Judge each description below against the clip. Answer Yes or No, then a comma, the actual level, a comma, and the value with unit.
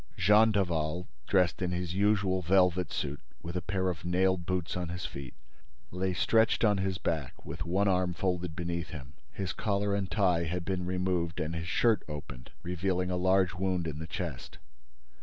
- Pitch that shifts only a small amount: Yes, narrow, 2.0 semitones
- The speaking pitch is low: Yes, very low, 90 Hz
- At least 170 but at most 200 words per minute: Yes, average, 180 wpm